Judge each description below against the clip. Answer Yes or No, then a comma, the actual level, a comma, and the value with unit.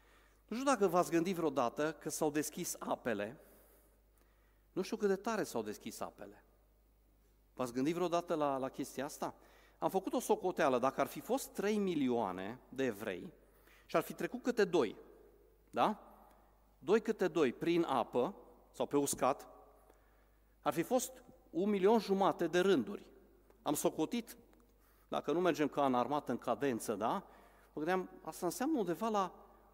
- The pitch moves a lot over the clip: Yes, wide, 6.6 semitones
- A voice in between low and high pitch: Yes, medium, 170 Hz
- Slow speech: No, average, 155 wpm